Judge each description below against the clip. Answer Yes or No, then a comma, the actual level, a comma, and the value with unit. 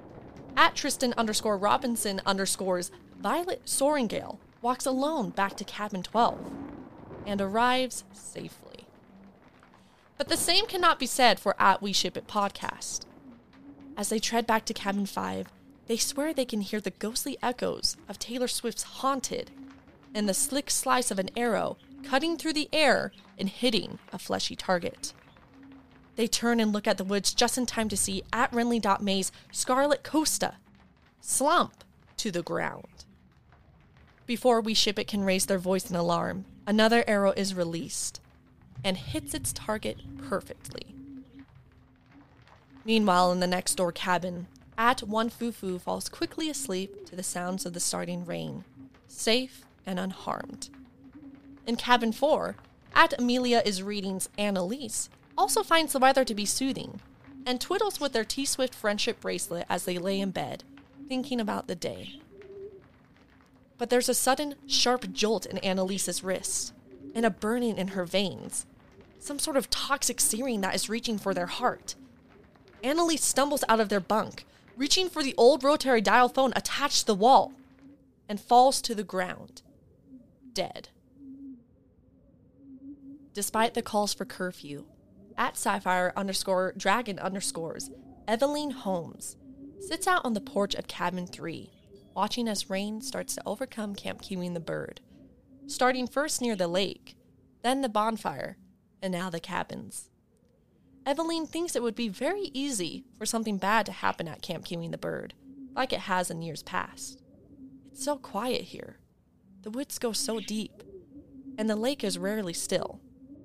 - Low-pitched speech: No, high, 225 Hz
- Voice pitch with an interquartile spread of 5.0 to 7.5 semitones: Yes, wide, 5.6 semitones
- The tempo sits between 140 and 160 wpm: Yes, average, 150 wpm